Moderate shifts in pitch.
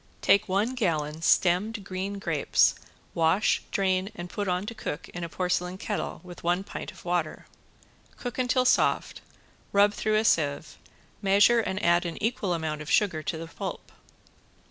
Yes: average, 3.2 semitones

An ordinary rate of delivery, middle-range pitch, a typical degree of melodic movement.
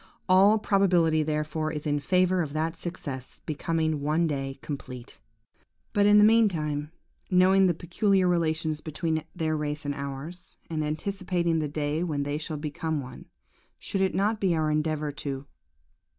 Yes: average, 155 wpm; medium, 160 Hz; average, 3.4 semitones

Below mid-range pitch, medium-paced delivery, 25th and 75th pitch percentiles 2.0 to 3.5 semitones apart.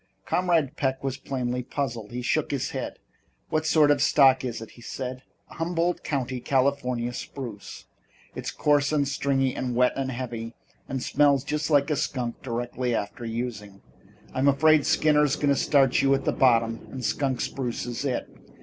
Yes: low, 130 Hz; average, 175 wpm; average, 2.7 semitones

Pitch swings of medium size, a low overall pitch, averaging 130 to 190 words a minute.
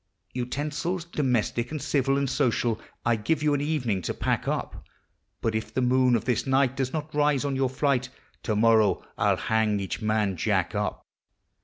Yes: average, 4.3 semitones; low, 130 Hz; average, 185 wpm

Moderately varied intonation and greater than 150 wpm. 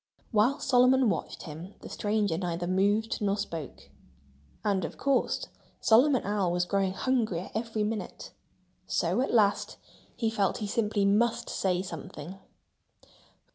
No: average, 3.3 semitones; slow, 135 wpm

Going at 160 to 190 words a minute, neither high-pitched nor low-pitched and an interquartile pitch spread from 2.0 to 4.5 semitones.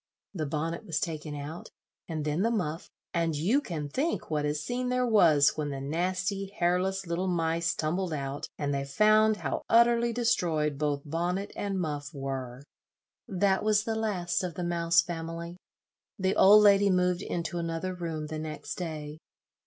Yes: average, 170 wpm; medium, 170 Hz; average, 4.2 semitones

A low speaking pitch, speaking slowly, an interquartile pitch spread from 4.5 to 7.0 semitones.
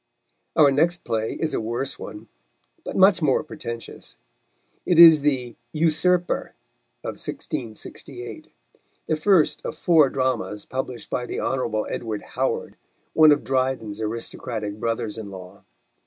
Yes: low, 130 Hz; slow, 130 wpm; wide, 5.6 semitones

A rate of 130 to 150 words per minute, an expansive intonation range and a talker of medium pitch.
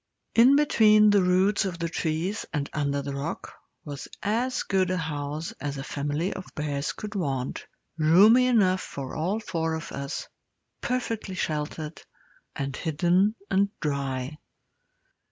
Yes: average, 140 wpm; wide, 5.7 semitones; medium, 165 Hz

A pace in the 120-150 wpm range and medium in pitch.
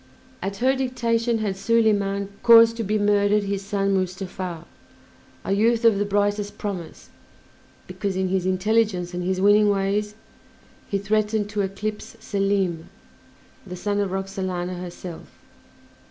No: slow, 135 wpm; high, 200 Hz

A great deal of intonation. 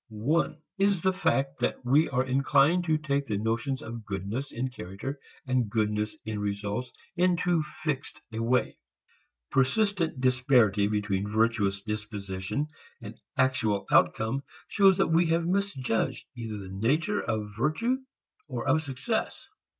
Yes: wide, 6.3 semitones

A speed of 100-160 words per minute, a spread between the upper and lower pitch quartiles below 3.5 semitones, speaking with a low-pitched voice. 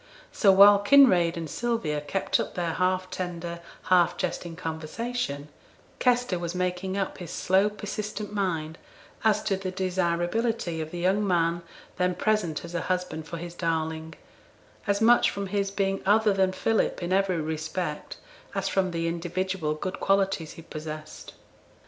No: average, 155 wpm; average, 3.0 semitones; medium, 185 Hz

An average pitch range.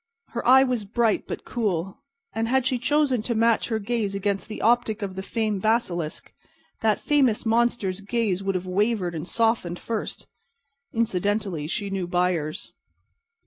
Yes: average, 3.7 semitones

